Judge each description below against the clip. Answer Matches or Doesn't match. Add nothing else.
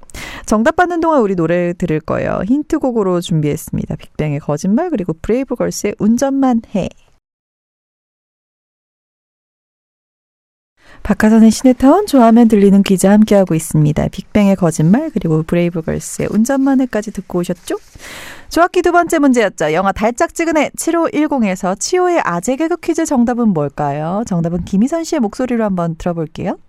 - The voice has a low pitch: Doesn't match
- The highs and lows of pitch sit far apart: Matches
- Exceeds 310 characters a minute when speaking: Matches